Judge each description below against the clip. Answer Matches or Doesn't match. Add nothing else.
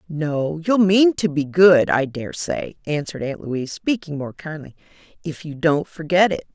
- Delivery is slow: Doesn't match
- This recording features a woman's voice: Matches